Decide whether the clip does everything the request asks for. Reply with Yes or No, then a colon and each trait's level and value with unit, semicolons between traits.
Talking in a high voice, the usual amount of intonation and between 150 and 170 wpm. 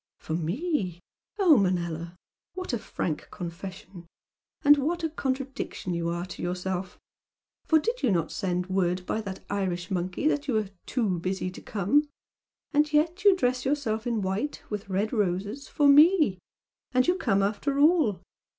No: high, 205 Hz; wide, 8.0 semitones; average, 160 wpm